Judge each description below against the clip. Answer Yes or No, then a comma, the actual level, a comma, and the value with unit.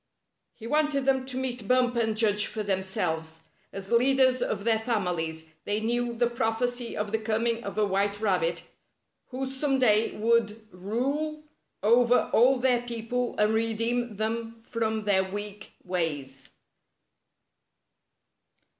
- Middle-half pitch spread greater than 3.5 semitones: No, average, 3.0 semitones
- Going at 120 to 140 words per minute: Yes, slow, 135 wpm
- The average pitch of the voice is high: Yes, high, 225 Hz